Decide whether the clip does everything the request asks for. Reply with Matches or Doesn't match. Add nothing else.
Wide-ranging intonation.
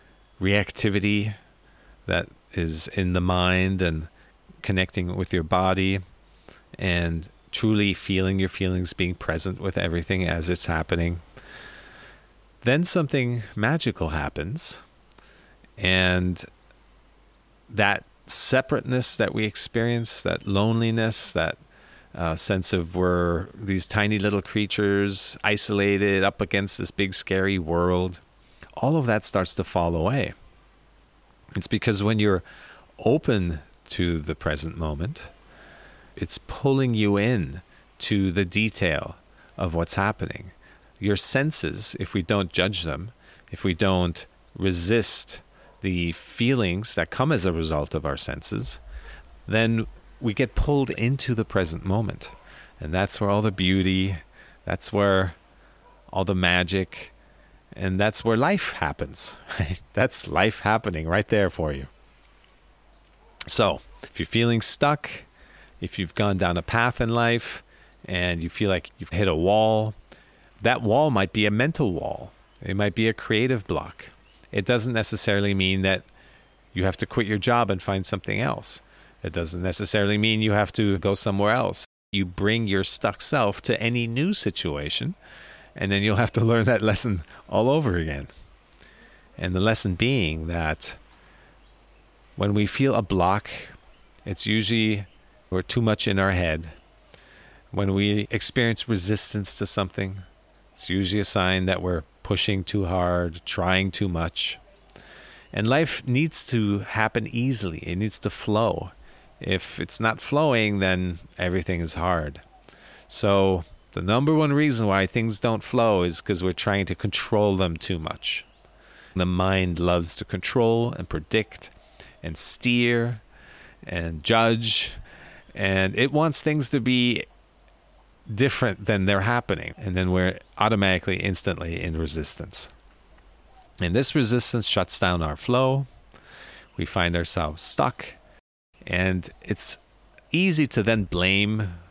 Doesn't match